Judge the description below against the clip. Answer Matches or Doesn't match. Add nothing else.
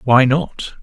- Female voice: Doesn't match